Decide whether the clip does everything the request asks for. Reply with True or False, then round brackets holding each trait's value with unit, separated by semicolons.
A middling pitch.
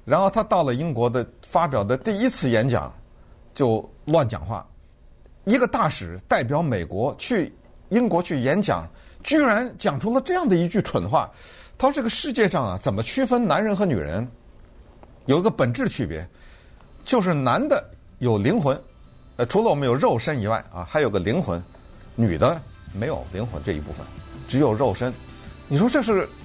False (120 Hz)